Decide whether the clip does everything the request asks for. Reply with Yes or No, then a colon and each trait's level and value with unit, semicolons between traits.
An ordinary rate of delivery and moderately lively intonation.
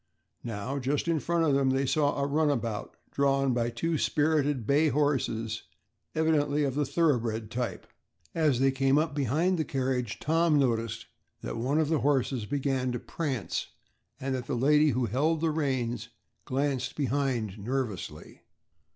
Yes: average, 155 wpm; average, 3.4 semitones